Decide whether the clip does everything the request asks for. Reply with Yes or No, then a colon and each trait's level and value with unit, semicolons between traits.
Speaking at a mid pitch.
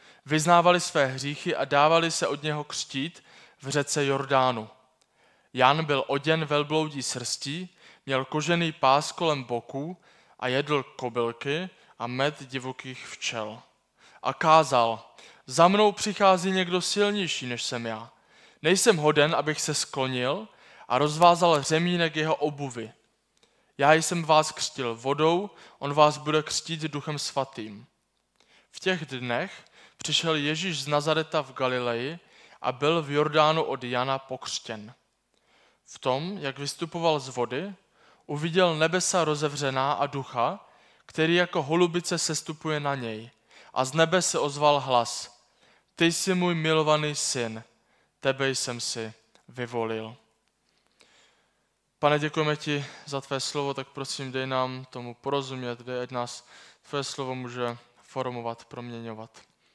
Yes: medium, 145 Hz